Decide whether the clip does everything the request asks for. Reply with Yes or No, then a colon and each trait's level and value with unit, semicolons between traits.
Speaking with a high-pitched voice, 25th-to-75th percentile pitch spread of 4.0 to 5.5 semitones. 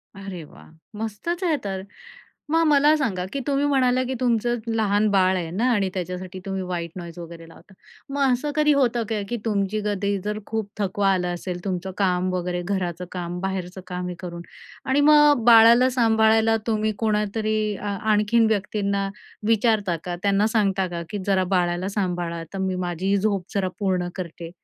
No: high, 200 Hz; average, 3.6 semitones